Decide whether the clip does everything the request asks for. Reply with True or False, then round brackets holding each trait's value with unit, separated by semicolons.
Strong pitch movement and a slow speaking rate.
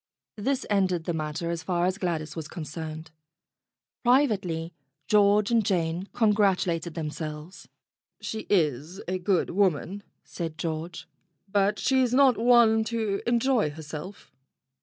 False (4.7 semitones; 125 wpm)